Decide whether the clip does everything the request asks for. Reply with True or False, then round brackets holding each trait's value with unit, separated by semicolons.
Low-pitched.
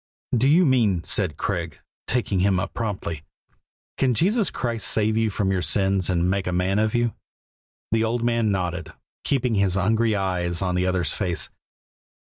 True (100 Hz)